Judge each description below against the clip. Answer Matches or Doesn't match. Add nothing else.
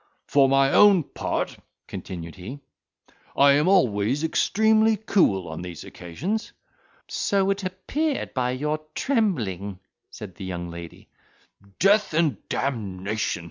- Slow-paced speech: Matches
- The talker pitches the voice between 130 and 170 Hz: Matches